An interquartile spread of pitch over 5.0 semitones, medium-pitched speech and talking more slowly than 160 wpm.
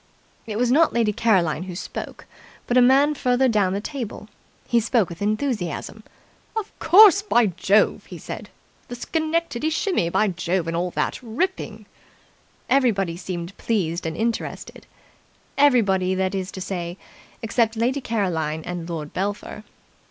No: wide, 5.5 semitones; high, 215 Hz; average, 145 wpm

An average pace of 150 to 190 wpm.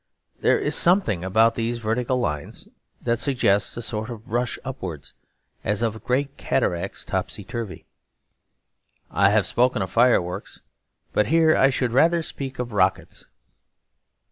No: average, 140 wpm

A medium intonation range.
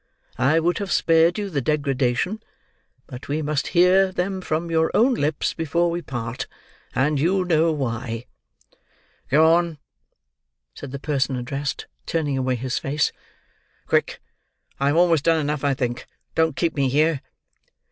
Yes: average, 3.7 semitones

